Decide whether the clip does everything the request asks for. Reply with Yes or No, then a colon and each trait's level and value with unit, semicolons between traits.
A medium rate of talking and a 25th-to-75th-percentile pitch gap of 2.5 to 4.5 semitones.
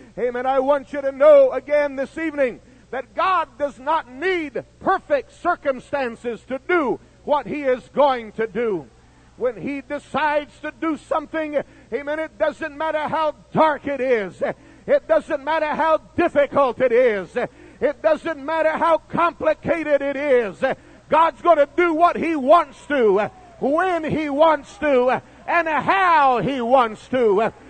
Yes: average, 150 wpm; average, 2.9 semitones